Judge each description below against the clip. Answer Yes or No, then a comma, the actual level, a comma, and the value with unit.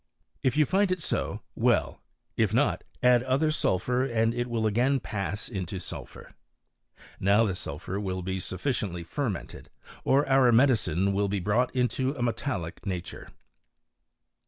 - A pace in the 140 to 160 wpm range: Yes, average, 150 wpm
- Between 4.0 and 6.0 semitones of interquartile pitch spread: Yes, average, 5.2 semitones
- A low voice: Yes, low, 115 Hz